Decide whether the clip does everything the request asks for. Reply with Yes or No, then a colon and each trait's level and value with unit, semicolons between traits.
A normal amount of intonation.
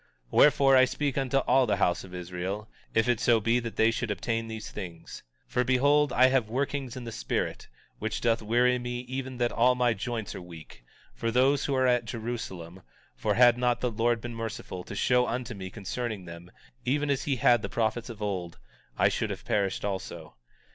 Yes: average, 3.2 semitones